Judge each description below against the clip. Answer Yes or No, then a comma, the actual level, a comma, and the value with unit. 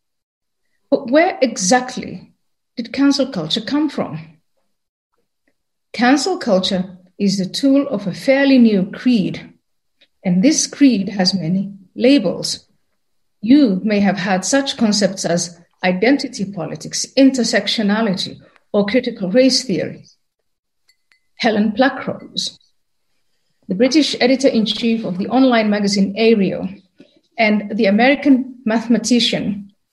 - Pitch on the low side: No, high, 225 Hz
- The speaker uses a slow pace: Yes, slow, 105 wpm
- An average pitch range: Yes, average, 5.0 semitones